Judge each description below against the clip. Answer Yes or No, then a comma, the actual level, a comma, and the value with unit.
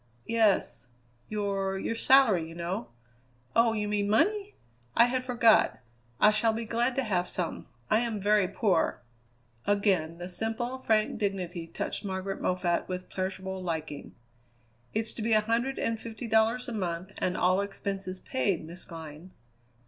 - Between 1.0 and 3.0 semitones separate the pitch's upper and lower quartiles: No, average, 3.7 semitones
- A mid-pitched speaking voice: No, high, 205 Hz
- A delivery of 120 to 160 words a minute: Yes, average, 155 wpm